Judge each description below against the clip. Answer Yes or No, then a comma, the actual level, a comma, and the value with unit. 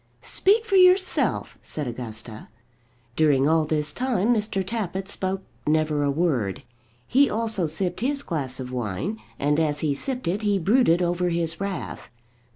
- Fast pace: No, average, 155 wpm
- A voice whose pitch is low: No, medium, 175 Hz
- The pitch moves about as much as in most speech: No, wide, 6.6 semitones